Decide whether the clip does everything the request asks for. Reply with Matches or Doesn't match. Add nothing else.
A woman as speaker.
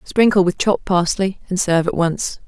Matches